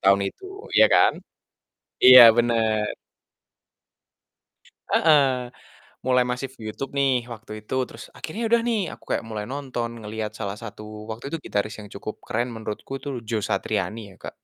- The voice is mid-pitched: No, low, 120 Hz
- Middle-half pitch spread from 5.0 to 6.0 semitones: No, average, 3.7 semitones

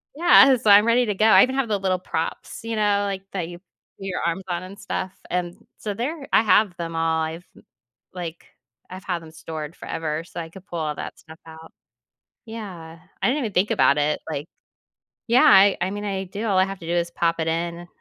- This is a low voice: No, medium, 185 Hz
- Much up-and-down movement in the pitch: No, average, 3.9 semitones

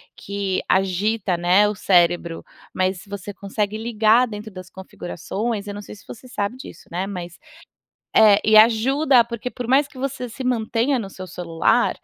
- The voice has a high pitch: Yes, high, 210 Hz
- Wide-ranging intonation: No, average, 3.8 semitones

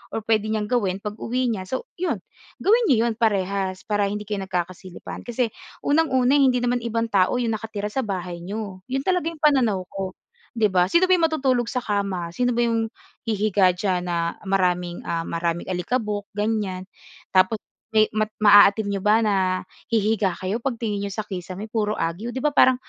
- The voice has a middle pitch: No, high, 210 Hz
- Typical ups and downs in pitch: Yes, average, 4.0 semitones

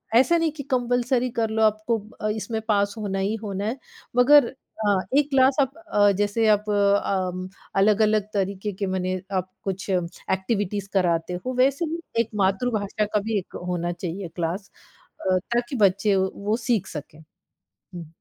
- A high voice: Yes, high, 205 Hz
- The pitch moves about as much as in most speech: Yes, average, 3.6 semitones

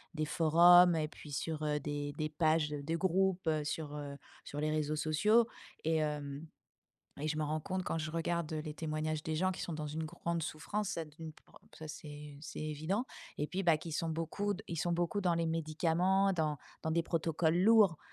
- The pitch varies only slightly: Yes, narrow, 2.1 semitones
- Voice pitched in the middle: Yes, medium, 160 Hz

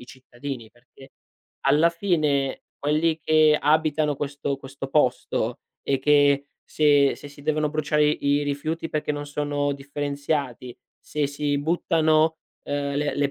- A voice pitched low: No, medium, 145 Hz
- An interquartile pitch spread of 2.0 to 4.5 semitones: No, narrow, 1.5 semitones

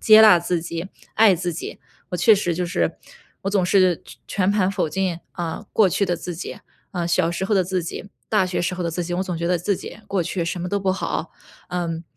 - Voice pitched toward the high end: No, medium, 180 Hz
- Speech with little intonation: Yes, narrow, 2.0 semitones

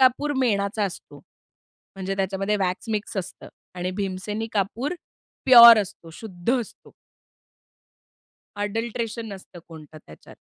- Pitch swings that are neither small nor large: Yes, average, 3.4 semitones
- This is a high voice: Yes, high, 200 Hz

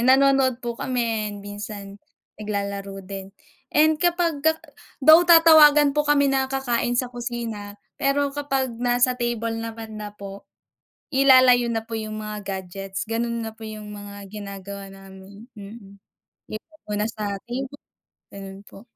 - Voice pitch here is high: Yes, high, 230 Hz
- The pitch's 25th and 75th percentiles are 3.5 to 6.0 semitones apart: Yes, average, 4.6 semitones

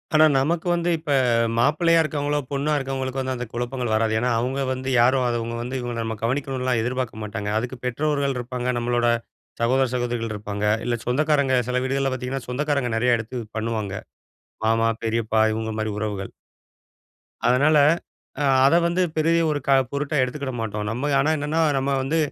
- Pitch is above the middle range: No, low, 125 Hz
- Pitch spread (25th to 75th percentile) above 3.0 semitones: Yes, average, 3.4 semitones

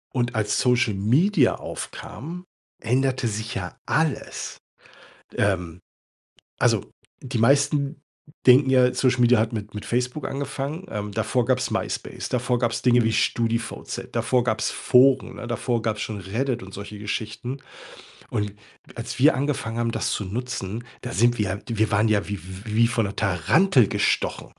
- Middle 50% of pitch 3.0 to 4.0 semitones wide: Yes, average, 3.3 semitones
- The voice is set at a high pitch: No, low, 120 Hz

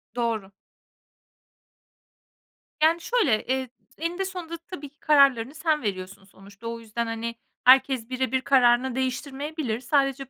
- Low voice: No, very high, 260 Hz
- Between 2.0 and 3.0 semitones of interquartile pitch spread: No, average, 4.3 semitones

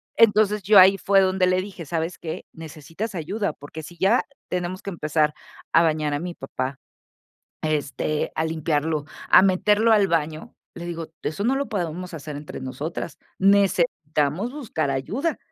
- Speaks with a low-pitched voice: No, medium, 170 Hz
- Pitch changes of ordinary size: Yes, average, 4.3 semitones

